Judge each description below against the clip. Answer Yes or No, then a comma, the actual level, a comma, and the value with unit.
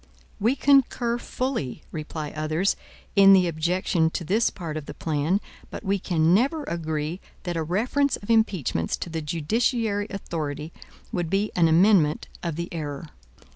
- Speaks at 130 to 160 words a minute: Yes, average, 155 wpm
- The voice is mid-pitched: Yes, medium, 175 Hz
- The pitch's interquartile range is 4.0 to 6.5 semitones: Yes, average, 4.6 semitones